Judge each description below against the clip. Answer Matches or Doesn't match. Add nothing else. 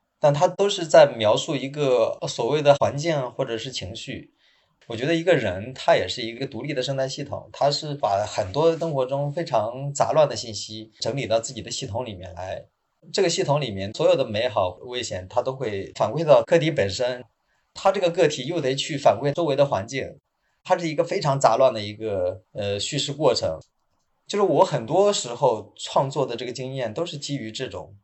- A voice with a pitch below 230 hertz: Matches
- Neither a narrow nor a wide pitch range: Matches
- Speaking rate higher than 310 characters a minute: Doesn't match